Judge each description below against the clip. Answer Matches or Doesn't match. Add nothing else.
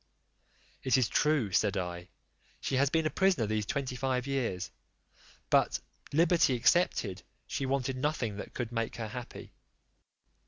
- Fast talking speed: Doesn't match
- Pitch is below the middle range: Matches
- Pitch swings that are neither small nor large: Matches